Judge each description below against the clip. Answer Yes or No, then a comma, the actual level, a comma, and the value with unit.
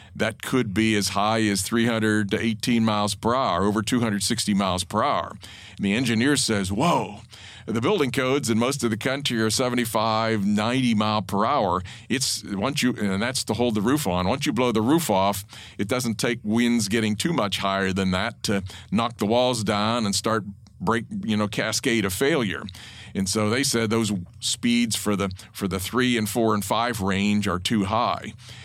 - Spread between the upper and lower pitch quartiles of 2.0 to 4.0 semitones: Yes, average, 2.7 semitones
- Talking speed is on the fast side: No, average, 195 wpm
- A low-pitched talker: Yes, low, 110 Hz